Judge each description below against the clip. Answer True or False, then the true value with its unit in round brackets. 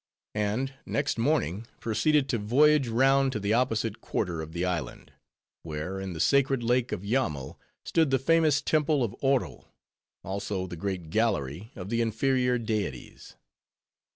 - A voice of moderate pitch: False (115 Hz)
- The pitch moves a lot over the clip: True (5.8 semitones)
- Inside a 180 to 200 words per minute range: False (150 wpm)